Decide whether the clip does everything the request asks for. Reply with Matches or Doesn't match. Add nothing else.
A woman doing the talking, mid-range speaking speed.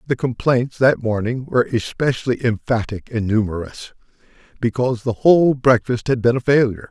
Doesn't match